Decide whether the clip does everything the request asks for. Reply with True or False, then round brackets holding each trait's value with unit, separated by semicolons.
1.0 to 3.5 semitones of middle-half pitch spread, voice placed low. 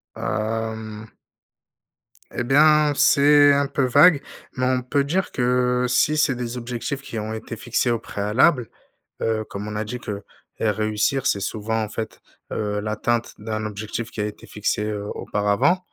False (3.9 semitones; 115 Hz)